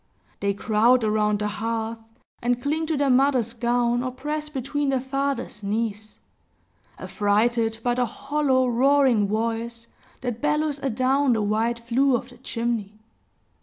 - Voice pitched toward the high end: Yes, high, 240 Hz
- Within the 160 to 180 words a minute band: No, average, 145 wpm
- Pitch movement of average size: Yes, average, 3.4 semitones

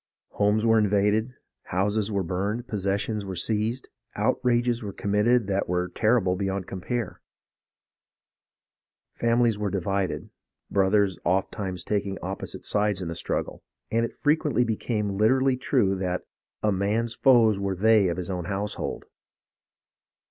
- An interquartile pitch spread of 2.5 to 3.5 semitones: Yes, average, 2.9 semitones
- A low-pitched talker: Yes, low, 105 Hz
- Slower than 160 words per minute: Yes, slow, 135 wpm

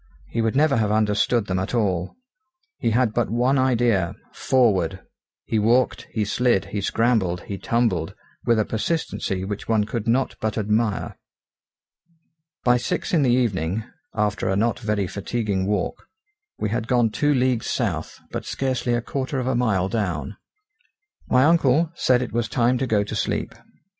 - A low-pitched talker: Yes, low, 115 Hz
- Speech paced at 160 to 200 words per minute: Yes, average, 165 wpm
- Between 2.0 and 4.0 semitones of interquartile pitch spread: Yes, average, 3.5 semitones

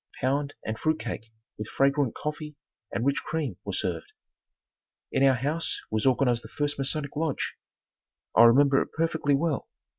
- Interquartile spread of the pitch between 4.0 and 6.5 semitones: No, average, 3.2 semitones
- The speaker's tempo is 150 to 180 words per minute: Yes, average, 155 wpm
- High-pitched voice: No, medium, 140 Hz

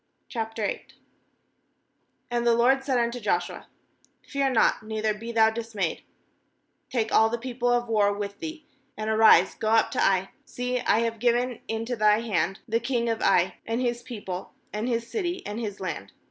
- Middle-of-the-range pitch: No, high, 230 Hz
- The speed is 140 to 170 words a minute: No, average, 180 wpm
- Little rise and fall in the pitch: Yes, narrow, 2.3 semitones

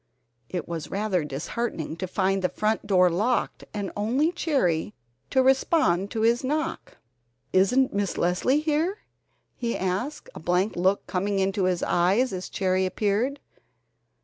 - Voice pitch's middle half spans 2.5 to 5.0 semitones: No, wide, 5.5 semitones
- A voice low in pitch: No, high, 200 Hz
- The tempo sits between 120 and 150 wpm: Yes, average, 145 wpm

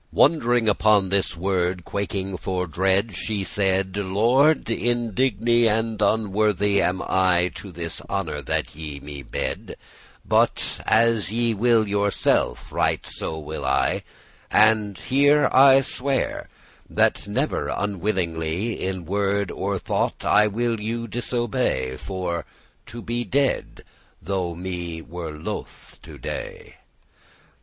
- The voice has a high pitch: No, low, 100 Hz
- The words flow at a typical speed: No, slow, 125 wpm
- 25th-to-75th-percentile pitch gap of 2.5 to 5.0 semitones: Yes, average, 4.3 semitones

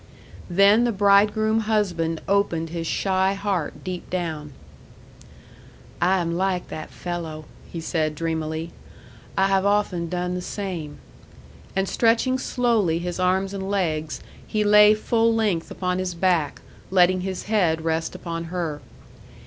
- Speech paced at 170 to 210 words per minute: No, slow, 135 wpm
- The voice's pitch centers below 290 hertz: Yes, medium, 185 Hz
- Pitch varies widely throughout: No, average, 3.3 semitones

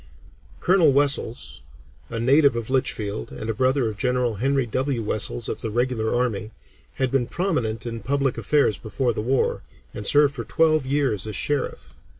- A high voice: No, low, 125 Hz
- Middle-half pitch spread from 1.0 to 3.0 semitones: No, average, 3.9 semitones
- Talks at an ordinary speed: Yes, average, 165 wpm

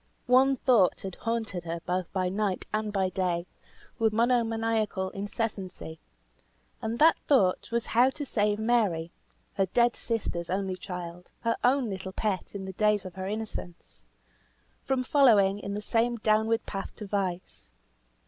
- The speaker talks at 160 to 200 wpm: No, average, 150 wpm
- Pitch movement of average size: Yes, average, 3.5 semitones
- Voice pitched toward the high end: Yes, high, 210 Hz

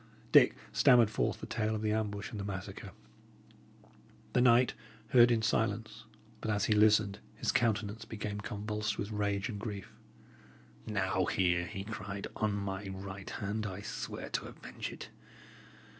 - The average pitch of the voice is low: Yes, low, 105 Hz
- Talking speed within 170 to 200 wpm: No, average, 155 wpm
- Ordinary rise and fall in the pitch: No, narrow, 1.7 semitones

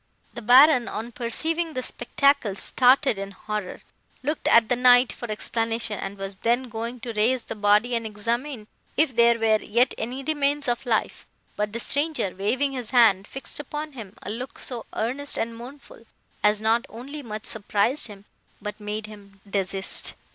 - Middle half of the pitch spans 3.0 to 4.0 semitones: Yes, average, 3.5 semitones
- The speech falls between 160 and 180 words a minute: Yes, average, 170 wpm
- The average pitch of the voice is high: Yes, high, 235 Hz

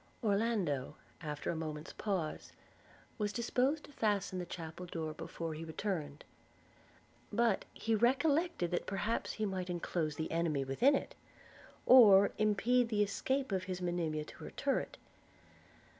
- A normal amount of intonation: No, wide, 5.8 semitones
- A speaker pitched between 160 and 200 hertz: Yes, high, 190 Hz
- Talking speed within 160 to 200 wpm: No, average, 140 wpm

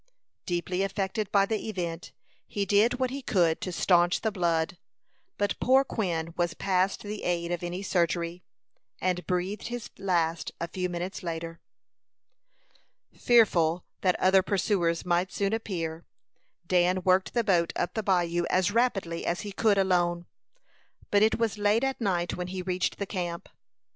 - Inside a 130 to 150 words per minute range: No, average, 160 wpm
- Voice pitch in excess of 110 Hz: Yes, medium, 185 Hz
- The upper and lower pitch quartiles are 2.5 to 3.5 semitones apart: Yes, average, 2.9 semitones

